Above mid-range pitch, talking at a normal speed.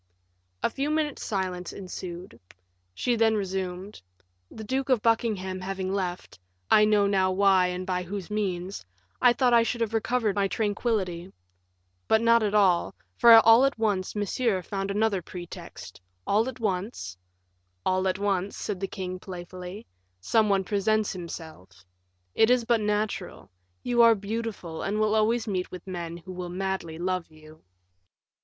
Yes: high, 195 Hz; average, 160 wpm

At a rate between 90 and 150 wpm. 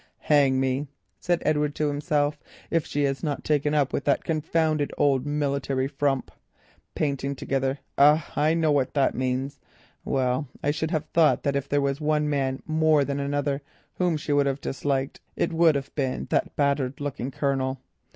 No: average, 175 wpm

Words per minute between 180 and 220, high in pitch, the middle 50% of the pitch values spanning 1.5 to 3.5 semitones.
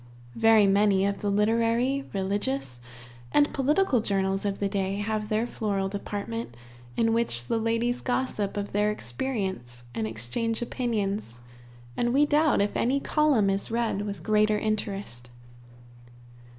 No: slow, 135 wpm; high, 210 Hz; average, 3.0 semitones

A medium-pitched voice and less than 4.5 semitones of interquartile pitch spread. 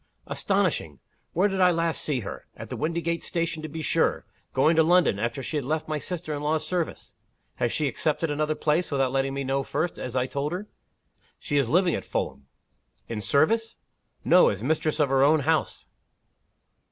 Yes: medium, 155 Hz; average, 3.6 semitones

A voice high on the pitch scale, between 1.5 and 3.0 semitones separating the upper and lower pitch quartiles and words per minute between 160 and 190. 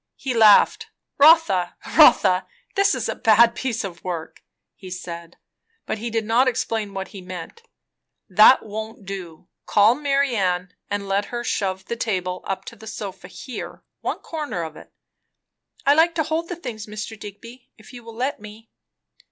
No: high, 215 Hz; average, 4.4 semitones; average, 170 wpm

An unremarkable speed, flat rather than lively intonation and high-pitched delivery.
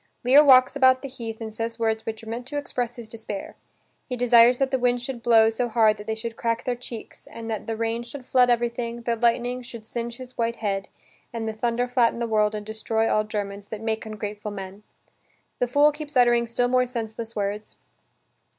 No: fast, 215 wpm; narrow, 1.9 semitones; high, 230 Hz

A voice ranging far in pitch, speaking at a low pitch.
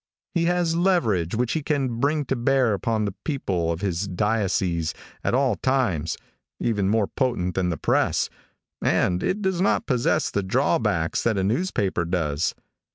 Yes: wide, 7.3 semitones; low, 110 Hz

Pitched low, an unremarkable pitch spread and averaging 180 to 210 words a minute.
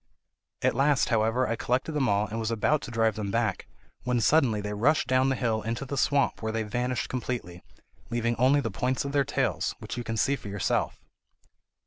Yes: low, 120 Hz; average, 3.1 semitones; fast, 205 wpm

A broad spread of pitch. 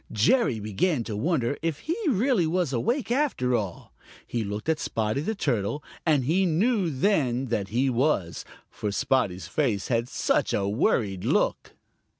Yes: wide, 8.0 semitones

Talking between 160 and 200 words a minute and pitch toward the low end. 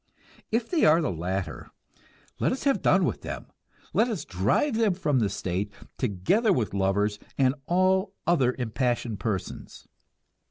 No: average, 150 wpm; low, 130 Hz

